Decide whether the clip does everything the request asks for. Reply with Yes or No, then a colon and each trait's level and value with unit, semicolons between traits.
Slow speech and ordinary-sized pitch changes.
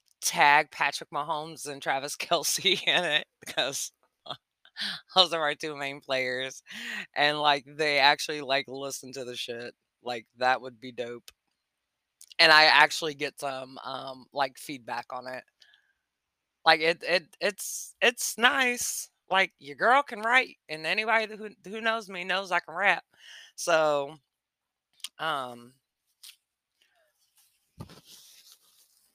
No: slow, 130 wpm; wide, 6.2 semitones